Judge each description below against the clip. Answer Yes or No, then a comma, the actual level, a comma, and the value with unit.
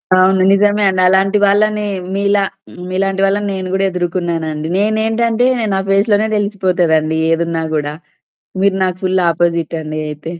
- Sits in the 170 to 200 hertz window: Yes, high, 190 Hz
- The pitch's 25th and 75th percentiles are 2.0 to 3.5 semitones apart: Yes, average, 3.2 semitones